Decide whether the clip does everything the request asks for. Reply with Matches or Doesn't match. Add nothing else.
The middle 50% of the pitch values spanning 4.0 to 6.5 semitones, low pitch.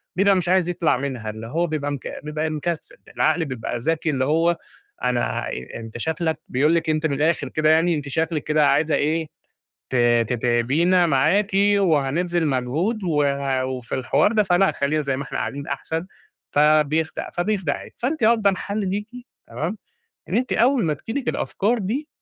Doesn't match